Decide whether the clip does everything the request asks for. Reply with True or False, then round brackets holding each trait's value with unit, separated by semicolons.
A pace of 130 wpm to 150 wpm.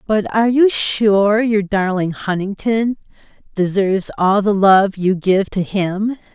True (140 wpm)